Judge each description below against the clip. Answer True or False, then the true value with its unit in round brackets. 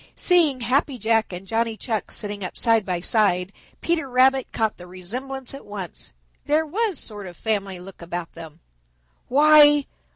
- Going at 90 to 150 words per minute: False (160 wpm)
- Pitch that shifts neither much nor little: False (6.2 semitones)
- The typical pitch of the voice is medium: False (225 Hz)